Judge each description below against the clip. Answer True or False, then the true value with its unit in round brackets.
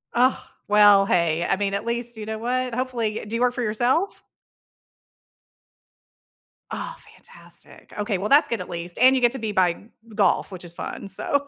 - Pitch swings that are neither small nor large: True (3.9 semitones)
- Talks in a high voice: True (220 Hz)